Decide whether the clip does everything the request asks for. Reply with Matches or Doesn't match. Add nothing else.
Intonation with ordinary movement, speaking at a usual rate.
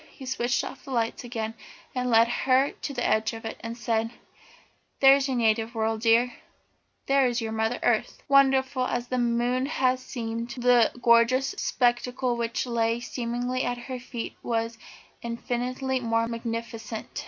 Doesn't match